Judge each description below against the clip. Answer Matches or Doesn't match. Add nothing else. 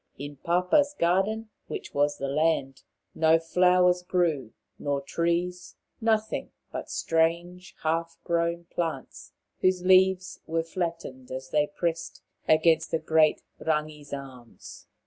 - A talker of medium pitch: Matches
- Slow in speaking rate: Matches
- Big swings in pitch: Doesn't match